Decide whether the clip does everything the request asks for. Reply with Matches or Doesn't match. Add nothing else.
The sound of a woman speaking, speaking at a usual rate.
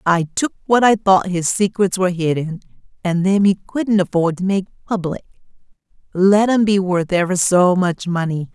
Matches